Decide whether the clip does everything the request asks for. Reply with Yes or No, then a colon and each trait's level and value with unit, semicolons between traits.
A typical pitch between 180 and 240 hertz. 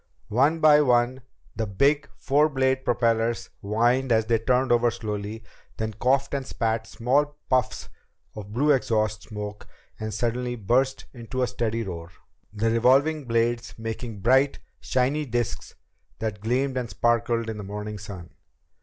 No: low, 120 Hz